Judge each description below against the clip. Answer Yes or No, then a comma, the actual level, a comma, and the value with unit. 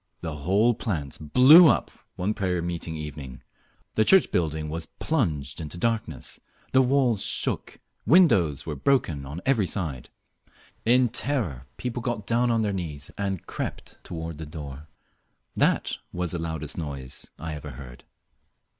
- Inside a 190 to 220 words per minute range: No, average, 145 wpm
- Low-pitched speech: Yes, very low, 85 Hz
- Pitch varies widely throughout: Yes, wide, 7.4 semitones